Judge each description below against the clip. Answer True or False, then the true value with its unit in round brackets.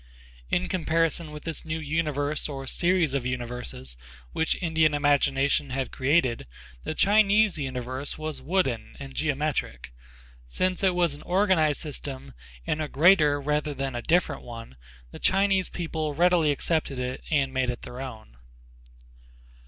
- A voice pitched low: False (150 Hz)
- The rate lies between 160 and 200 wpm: False (145 wpm)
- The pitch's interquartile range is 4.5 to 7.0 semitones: False (3.9 semitones)